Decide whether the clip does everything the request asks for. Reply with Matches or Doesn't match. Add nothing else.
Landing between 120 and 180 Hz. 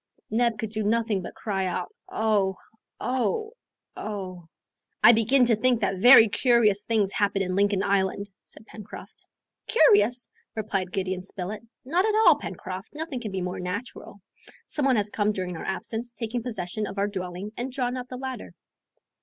Doesn't match